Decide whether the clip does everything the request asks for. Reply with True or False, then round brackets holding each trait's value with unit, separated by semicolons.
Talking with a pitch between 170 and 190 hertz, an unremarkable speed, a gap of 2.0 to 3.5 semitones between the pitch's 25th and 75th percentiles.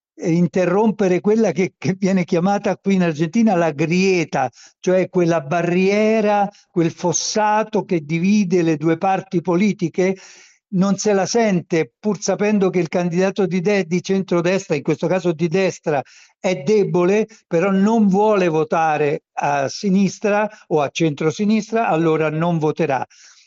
True (185 Hz; 140 wpm; 2.9 semitones)